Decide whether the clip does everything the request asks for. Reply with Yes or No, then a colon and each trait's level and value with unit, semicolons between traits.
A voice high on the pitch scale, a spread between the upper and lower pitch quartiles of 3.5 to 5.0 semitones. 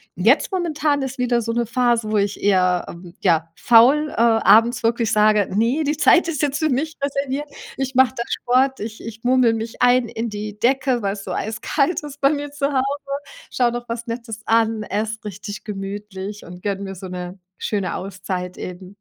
Yes: high, 230 Hz; average, 4.4 semitones